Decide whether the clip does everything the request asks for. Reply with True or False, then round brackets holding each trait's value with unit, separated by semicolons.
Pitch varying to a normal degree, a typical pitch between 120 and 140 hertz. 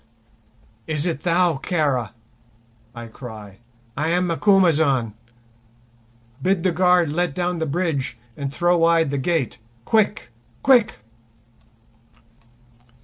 False (4.5 semitones; 165 Hz)